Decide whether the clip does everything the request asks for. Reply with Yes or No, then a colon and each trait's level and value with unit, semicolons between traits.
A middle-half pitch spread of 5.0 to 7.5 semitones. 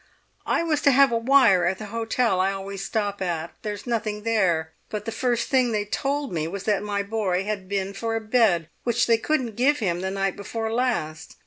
No: average, 3.4 semitones